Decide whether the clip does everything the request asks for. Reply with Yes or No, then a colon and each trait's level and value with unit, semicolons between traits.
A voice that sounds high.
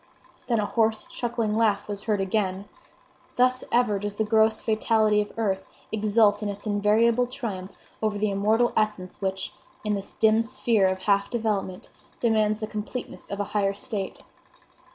Yes: high, 215 Hz